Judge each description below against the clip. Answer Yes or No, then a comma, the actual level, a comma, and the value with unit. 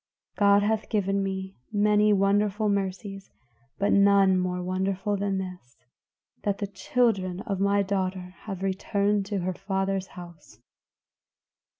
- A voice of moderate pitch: No, high, 195 Hz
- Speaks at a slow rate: Yes, slow, 125 wpm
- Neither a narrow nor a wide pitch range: No, narrow, 1.3 semitones